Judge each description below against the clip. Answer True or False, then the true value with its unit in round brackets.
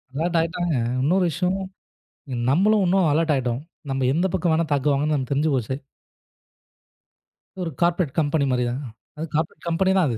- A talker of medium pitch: True (160 Hz)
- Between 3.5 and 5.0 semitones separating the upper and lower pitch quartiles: True (4.0 semitones)